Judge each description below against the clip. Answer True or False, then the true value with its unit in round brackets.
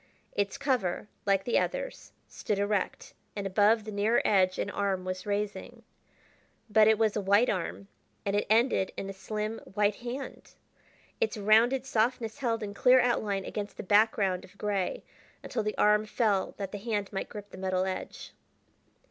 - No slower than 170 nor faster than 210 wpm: True (175 wpm)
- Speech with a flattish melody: True (2.3 semitones)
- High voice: True (210 Hz)